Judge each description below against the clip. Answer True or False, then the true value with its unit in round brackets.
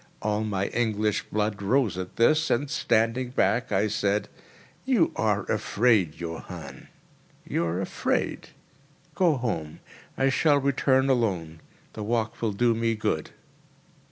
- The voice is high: False (110 Hz)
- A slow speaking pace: True (125 wpm)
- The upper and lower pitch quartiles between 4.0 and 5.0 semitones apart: True (4.4 semitones)